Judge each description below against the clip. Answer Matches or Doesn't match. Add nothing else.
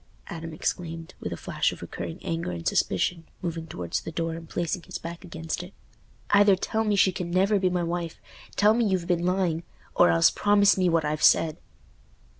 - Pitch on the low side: Doesn't match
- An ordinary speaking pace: Matches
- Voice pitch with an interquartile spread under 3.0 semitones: Matches